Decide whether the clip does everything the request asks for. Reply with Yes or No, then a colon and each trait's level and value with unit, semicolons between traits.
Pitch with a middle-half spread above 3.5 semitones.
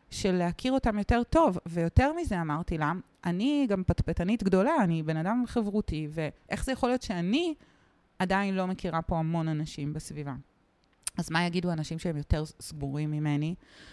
Yes: average, 5.3 semitones